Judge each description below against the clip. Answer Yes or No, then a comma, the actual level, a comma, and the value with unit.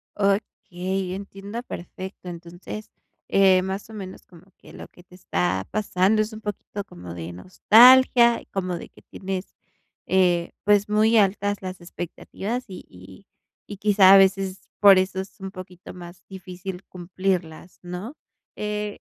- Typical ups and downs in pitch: No, narrow, 2.2 semitones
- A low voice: No, high, 190 Hz